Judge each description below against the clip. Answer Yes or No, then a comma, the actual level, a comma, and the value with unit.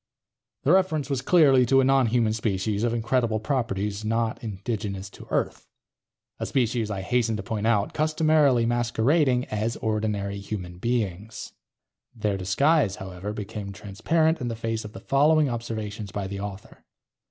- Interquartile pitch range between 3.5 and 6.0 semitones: Yes, average, 3.9 semitones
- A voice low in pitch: Yes, low, 110 Hz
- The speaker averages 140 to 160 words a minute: Yes, average, 150 wpm